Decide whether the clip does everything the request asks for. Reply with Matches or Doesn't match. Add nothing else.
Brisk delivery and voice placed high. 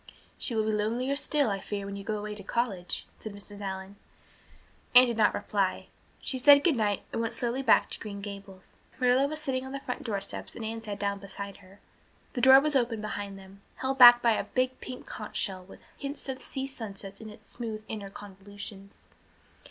Matches